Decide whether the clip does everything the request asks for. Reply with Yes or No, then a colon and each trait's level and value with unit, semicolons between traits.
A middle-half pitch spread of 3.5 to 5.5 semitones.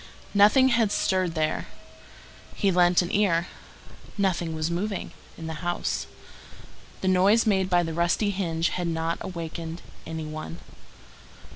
No: average, 3.0 semitones